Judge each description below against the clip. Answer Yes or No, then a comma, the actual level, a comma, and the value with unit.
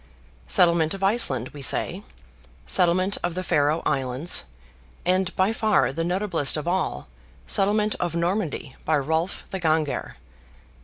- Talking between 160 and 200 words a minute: No, average, 140 wpm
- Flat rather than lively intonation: No, average, 4.1 semitones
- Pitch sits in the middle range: Yes, medium, 170 Hz